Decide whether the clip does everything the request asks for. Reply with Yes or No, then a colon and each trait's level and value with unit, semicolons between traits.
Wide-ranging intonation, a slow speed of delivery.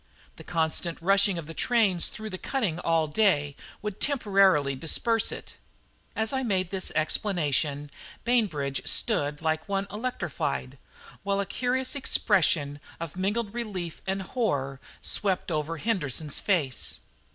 Yes: wide, 5.8 semitones; slow, 130 wpm